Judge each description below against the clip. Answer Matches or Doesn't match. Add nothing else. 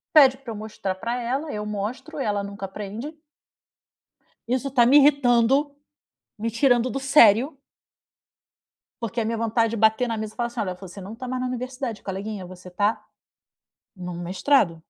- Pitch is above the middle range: Matches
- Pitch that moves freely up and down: Doesn't match